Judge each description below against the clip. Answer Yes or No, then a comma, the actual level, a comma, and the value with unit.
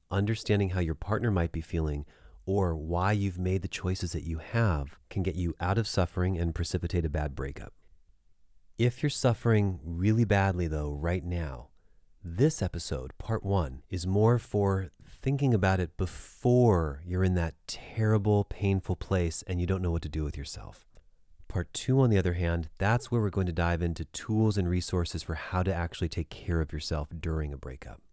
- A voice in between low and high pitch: No, very low, 90 Hz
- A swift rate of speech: No, average, 190 wpm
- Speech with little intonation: No, average, 3.8 semitones